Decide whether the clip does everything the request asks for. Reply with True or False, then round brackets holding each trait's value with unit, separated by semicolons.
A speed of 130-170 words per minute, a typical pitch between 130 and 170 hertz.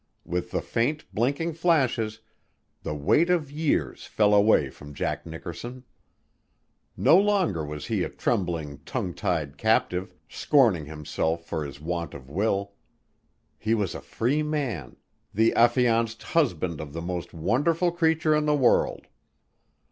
False (140 wpm; 110 Hz)